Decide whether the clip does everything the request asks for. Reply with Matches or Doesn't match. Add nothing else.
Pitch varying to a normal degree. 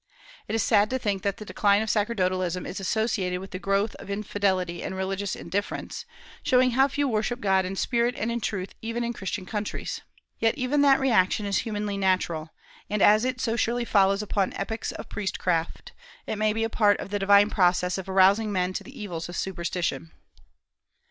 Matches